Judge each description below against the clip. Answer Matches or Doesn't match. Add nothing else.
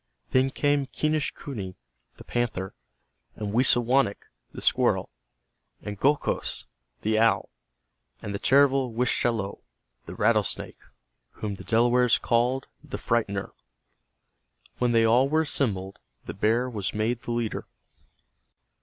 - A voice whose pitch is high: Doesn't match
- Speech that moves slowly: Matches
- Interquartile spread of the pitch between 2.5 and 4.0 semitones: Matches